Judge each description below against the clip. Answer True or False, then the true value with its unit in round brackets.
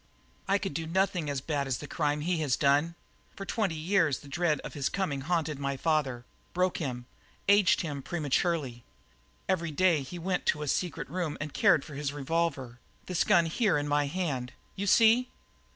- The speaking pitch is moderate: True (155 Hz)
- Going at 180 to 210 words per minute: True (185 wpm)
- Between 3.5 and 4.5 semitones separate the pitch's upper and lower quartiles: True (4.2 semitones)